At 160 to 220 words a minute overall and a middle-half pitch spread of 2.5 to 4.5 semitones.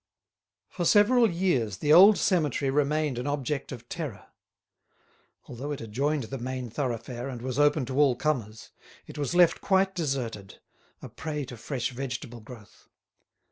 No: average, 150 wpm; average, 4.2 semitones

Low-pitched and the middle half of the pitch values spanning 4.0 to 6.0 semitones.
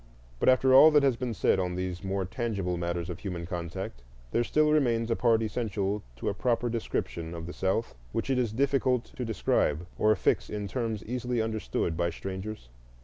Yes: low, 110 Hz; average, 5.2 semitones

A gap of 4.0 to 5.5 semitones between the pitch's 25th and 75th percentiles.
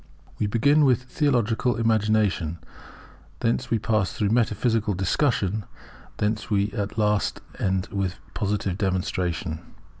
No: average, 2.7 semitones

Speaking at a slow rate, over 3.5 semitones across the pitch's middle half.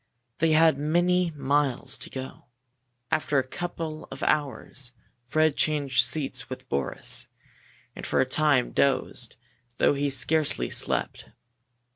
No: slow, 125 wpm; average, 2.9 semitones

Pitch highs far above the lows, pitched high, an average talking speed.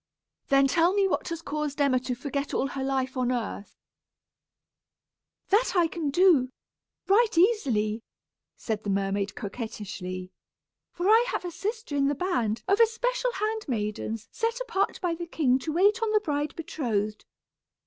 Yes: wide, 8.5 semitones; very high, 290 Hz; average, 160 wpm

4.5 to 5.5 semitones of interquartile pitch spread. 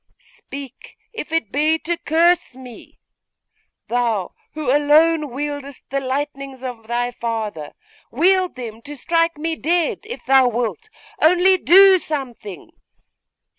Yes: average, 5.2 semitones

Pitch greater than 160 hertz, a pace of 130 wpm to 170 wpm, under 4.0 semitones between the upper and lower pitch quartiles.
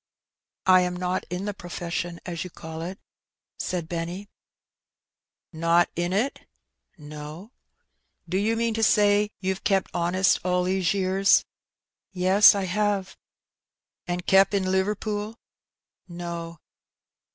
Yes: medium, 185 Hz; average, 150 wpm; narrow, 2.5 semitones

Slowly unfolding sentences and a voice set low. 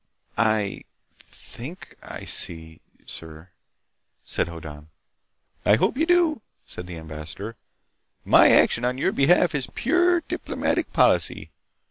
Yes: slow, 115 wpm; low, 110 Hz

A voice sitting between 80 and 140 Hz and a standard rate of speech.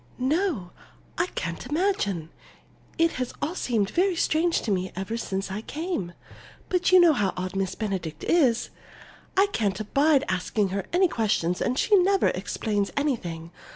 No: high, 230 Hz; average, 155 wpm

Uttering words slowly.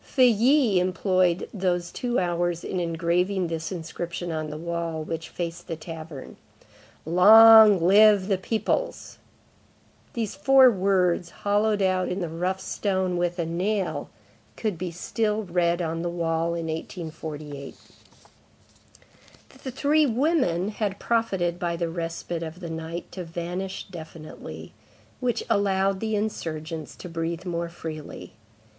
Yes: slow, 130 wpm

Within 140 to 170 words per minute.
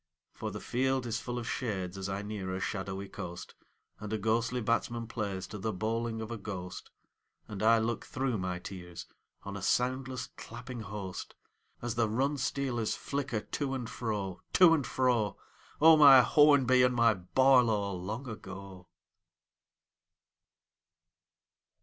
Yes: average, 150 wpm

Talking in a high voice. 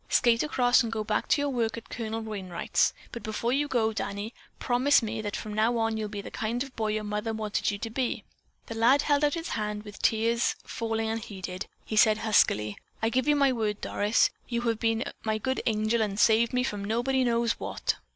Yes: high, 225 Hz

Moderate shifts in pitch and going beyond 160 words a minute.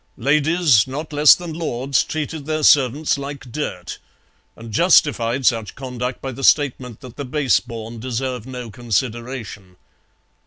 No: average, 3.8 semitones; average, 140 wpm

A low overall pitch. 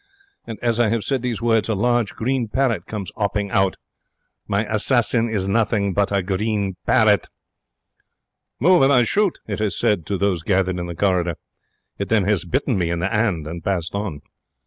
Yes: low, 105 Hz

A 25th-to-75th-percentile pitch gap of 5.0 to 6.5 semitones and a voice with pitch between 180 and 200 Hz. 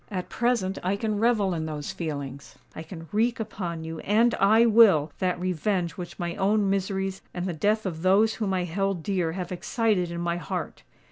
No: average, 3.4 semitones; high, 190 Hz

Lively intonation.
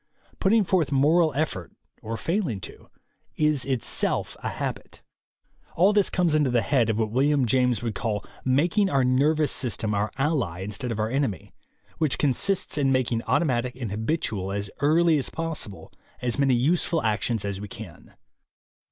Yes: wide, 5.7 semitones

